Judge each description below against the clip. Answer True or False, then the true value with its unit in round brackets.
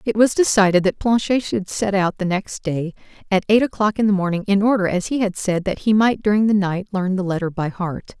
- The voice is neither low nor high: False (200 Hz)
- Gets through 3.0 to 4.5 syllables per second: False (5.5 syllables/s)